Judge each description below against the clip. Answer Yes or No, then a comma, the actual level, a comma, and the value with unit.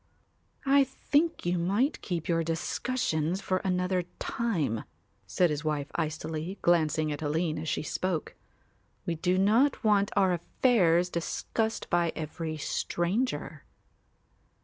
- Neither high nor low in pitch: Yes, medium, 175 Hz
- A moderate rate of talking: No, slow, 125 wpm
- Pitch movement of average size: Yes, average, 4.4 semitones